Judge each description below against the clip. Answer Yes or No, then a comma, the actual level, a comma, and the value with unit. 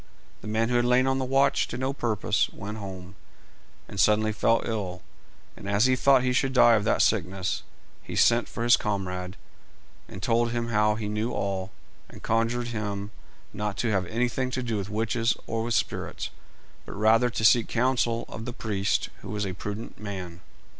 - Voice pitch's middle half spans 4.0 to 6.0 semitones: No, average, 2.9 semitones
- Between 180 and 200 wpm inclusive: Yes, average, 190 wpm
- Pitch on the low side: Yes, low, 110 Hz